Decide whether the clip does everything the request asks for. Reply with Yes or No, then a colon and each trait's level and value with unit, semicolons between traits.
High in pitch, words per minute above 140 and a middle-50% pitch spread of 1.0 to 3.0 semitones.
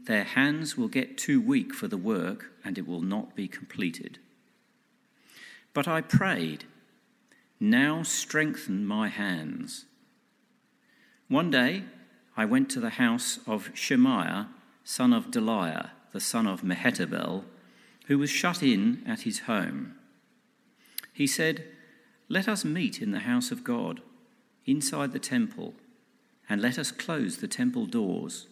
No: high, 240 Hz; slow, 135 wpm; narrow, 2.6 semitones